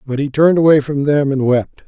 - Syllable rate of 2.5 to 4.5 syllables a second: No, 5.7 syllables/s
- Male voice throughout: Yes, male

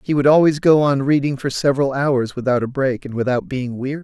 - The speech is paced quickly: Yes, fast, 240 wpm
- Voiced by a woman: No, male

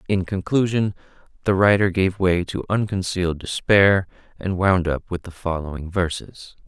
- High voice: No, very low, 95 Hz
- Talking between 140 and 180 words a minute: Yes, average, 145 wpm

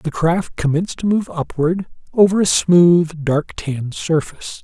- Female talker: No, male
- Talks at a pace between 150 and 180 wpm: Yes, average, 155 wpm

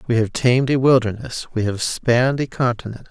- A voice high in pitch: No, low, 120 Hz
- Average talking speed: Yes, average, 195 wpm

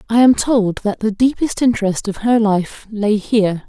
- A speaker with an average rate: Yes, average, 195 wpm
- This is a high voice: Yes, high, 215 Hz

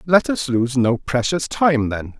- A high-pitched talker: No, medium, 140 Hz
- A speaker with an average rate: Yes, average, 190 wpm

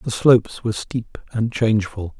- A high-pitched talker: No, low, 110 Hz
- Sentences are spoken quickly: No, average, 165 wpm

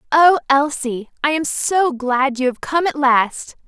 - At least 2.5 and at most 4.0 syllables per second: Yes, 3.8 syllables/s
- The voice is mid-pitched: No, very high, 280 Hz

